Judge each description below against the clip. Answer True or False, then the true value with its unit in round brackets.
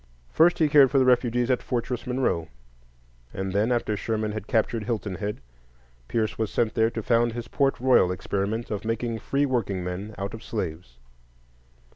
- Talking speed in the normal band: True (170 wpm)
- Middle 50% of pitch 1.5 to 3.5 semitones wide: True (3.2 semitones)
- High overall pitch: False (115 Hz)